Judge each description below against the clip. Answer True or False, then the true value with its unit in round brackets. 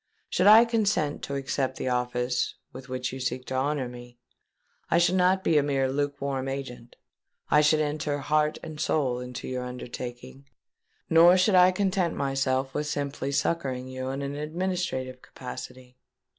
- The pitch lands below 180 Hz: True (140 Hz)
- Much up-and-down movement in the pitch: False (3.2 semitones)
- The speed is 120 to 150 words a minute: False (160 wpm)